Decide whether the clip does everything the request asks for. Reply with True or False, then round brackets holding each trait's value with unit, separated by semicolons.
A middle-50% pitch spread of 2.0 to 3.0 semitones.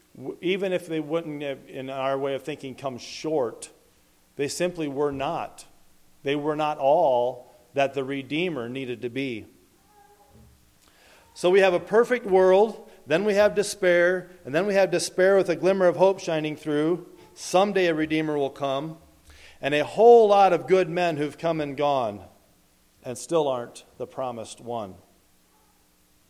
False (5.2 semitones)